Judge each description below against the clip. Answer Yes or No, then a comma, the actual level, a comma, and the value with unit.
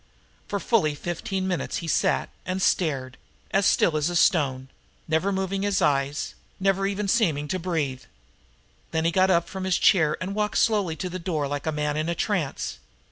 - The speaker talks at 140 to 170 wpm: No, average, 185 wpm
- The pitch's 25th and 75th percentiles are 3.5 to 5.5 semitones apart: Yes, average, 4.2 semitones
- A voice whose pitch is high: No, medium, 175 Hz